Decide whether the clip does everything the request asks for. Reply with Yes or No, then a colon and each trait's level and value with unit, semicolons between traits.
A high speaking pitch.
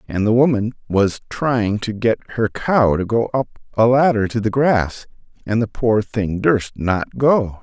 No: low, 115 Hz